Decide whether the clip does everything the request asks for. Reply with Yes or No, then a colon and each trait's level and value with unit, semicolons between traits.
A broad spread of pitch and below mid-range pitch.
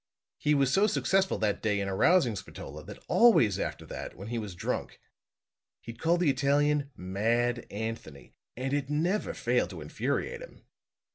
Yes: wide, 6.5 semitones; low, 130 Hz